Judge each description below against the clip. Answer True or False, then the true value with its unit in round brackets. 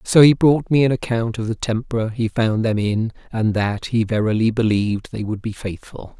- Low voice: True (115 Hz)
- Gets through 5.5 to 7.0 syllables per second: False (5.0 syllables/s)